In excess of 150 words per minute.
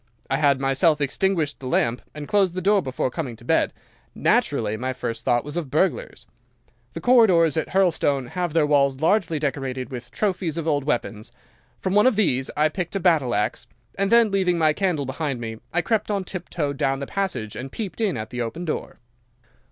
Yes: average, 200 wpm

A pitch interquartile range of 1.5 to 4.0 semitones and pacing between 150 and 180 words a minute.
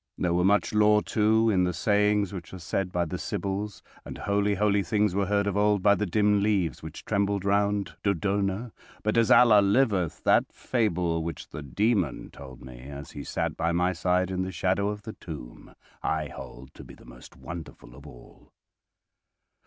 No: average, 3.5 semitones; average, 190 wpm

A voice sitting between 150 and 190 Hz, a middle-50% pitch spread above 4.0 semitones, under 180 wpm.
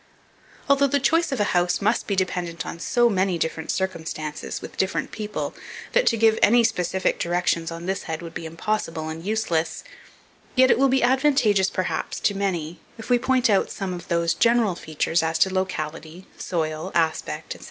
No: medium, 185 Hz; average, 5.2 semitones; average, 185 wpm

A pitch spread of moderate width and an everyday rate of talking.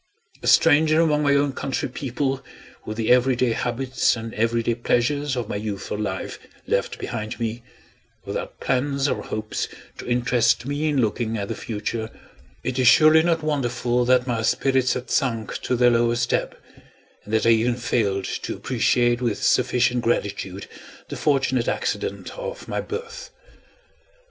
Yes: average, 3.1 semitones; average, 160 wpm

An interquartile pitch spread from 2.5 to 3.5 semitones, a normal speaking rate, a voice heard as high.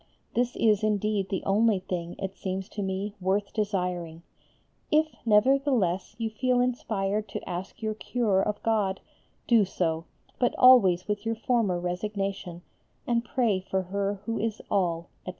Yes: average, 3.2 semitones; average, 150 wpm; high, 200 Hz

